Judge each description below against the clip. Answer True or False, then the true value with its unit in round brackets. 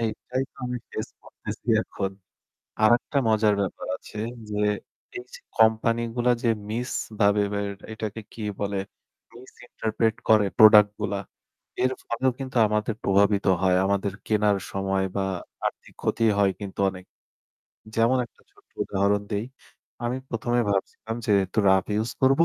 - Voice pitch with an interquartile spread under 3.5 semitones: True (2.5 semitones)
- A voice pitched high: False (110 Hz)